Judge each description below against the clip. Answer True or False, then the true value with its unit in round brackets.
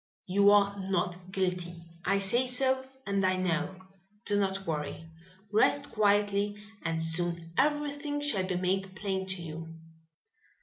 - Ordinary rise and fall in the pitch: False (2.3 semitones)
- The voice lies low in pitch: False (195 Hz)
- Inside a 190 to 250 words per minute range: False (135 wpm)